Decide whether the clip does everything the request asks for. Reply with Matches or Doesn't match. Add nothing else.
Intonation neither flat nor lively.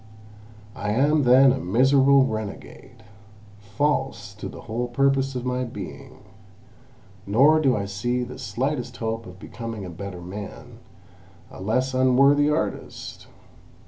Matches